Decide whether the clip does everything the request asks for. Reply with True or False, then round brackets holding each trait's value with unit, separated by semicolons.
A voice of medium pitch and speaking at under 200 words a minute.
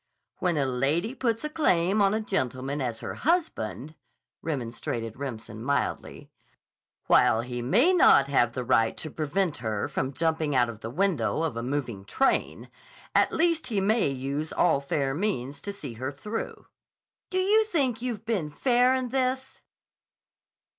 True (155 Hz; 160 wpm)